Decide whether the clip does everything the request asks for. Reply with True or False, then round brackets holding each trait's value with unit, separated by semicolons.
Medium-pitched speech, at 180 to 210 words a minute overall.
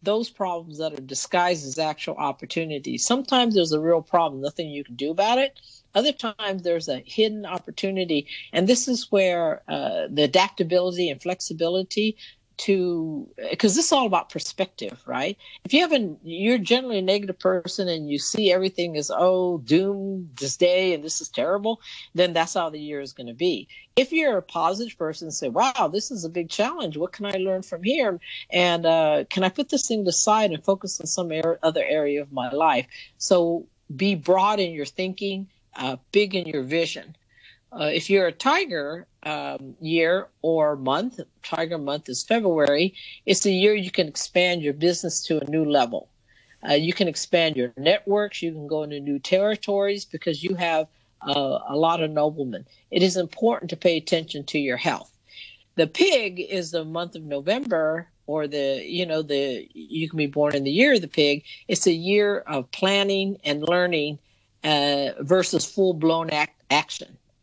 True (175 Hz; 185 wpm)